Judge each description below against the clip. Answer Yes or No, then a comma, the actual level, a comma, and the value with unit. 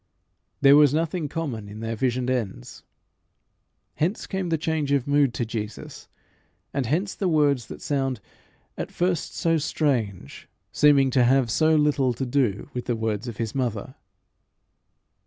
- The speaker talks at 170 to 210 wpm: No, average, 155 wpm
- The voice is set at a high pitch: No, low, 135 Hz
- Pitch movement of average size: Yes, average, 4.4 semitones